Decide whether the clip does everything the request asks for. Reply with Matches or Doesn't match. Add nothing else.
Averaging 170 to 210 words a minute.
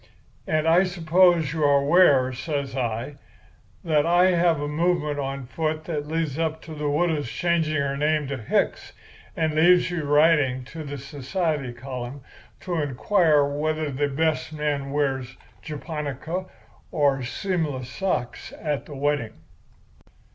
Doesn't match